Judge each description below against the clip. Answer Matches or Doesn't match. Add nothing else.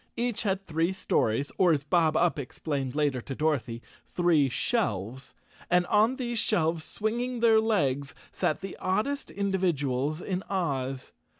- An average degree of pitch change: Doesn't match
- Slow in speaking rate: Doesn't match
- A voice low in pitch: Doesn't match